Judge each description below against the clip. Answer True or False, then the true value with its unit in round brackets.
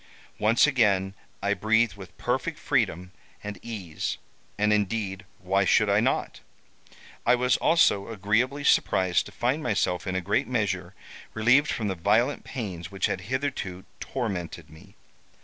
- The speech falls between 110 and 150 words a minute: True (140 wpm)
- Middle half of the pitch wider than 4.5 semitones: False (4.0 semitones)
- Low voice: True (105 Hz)